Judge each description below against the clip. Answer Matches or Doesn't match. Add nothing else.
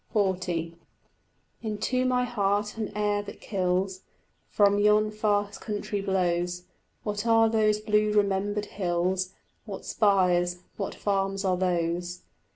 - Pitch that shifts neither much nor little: Doesn't match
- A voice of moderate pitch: Doesn't match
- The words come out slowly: Matches